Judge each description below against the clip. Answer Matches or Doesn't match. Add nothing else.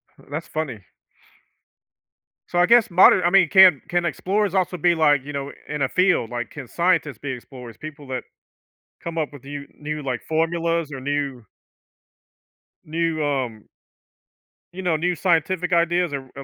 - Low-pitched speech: Doesn't match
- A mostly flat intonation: Doesn't match